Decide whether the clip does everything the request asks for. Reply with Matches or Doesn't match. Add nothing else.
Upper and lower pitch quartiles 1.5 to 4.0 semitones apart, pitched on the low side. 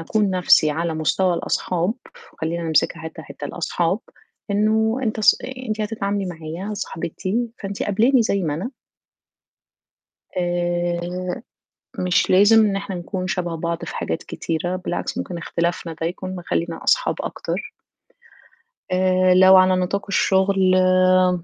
Doesn't match